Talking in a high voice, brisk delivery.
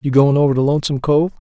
No: medium, 140 Hz; fast, 245 wpm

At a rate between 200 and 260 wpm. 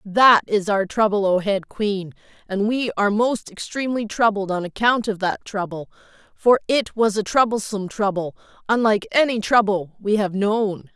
No: average, 165 wpm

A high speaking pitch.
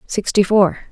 Yes: high, 200 Hz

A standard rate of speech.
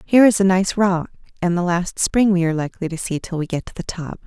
No: fast, 265 wpm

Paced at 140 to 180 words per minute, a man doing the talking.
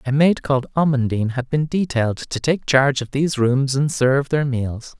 No: fast, 205 wpm; male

